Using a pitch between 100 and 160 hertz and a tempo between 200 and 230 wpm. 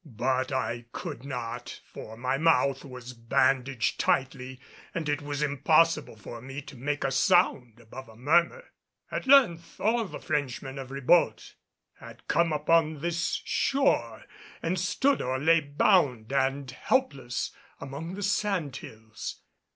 No: medium, 140 Hz; average, 140 wpm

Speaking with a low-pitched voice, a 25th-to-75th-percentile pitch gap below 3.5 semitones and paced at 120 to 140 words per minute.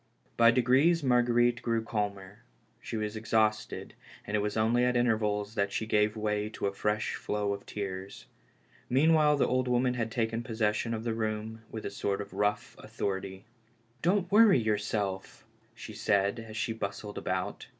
No: low, 110 Hz; narrow, 2.6 semitones; average, 170 wpm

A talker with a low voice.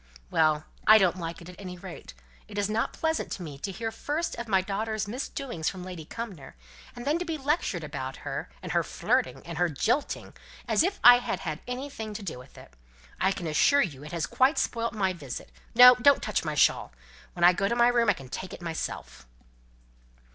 No: high, 200 Hz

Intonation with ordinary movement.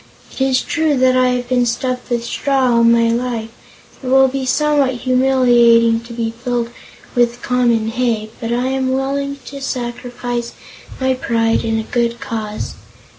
No: narrow, 1.9 semitones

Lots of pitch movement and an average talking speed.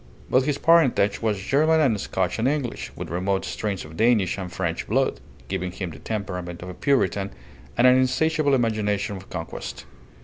Yes: wide, 5.7 semitones; average, 175 wpm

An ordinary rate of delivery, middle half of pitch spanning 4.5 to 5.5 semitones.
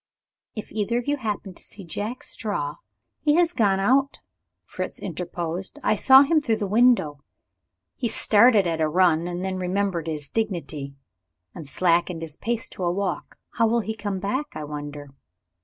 Yes: average, 175 wpm; average, 5.2 semitones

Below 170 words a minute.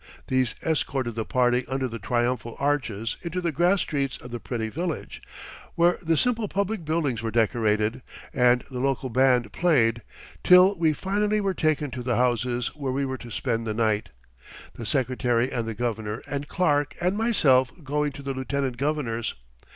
No: average, 175 wpm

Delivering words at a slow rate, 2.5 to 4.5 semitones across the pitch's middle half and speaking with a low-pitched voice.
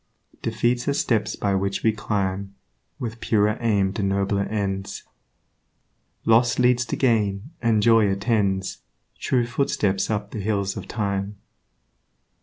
Yes: slow, 130 wpm; average, 2.8 semitones; low, 105 Hz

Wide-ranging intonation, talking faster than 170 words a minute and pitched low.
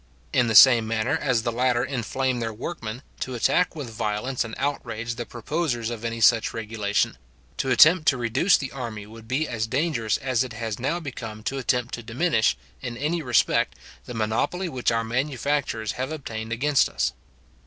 No: average, 3.2 semitones; average, 180 wpm; low, 120 Hz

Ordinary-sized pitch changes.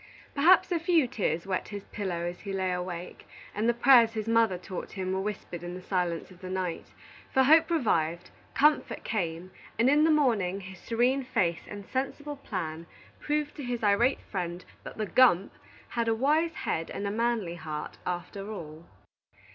No: wide, 6.0 semitones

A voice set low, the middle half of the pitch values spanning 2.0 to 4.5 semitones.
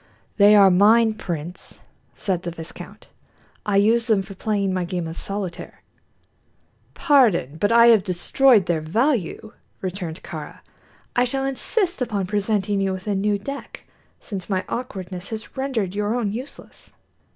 No: high, 205 Hz; average, 3.9 semitones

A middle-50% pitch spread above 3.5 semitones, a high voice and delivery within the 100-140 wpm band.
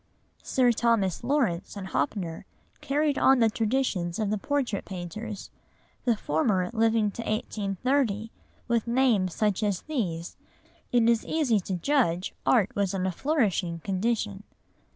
Yes: average, 4.1 semitones; high, 215 Hz; slow, 135 wpm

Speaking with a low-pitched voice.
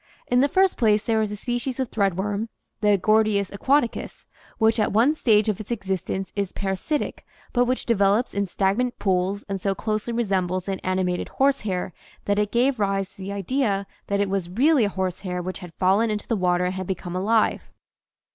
No: high, 205 Hz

